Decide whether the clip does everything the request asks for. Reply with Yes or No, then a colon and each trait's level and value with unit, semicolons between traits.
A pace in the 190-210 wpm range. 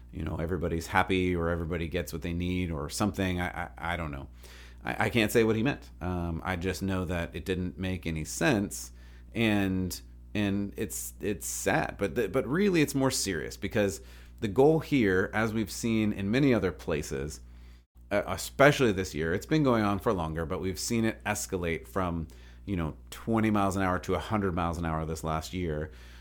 Yes: average, 195 wpm